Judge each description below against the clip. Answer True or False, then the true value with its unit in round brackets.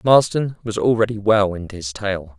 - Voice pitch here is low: True (105 Hz)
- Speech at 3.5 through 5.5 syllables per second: True (5.0 syllables/s)